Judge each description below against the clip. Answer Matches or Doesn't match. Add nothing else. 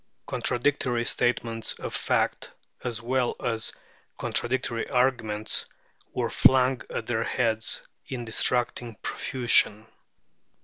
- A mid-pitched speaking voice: Doesn't match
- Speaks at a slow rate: Matches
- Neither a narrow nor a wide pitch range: Doesn't match